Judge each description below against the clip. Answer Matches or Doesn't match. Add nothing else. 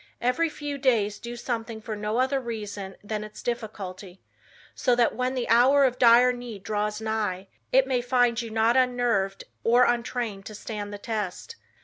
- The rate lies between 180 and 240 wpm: Doesn't match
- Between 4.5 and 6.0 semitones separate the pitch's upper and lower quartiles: Doesn't match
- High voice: Matches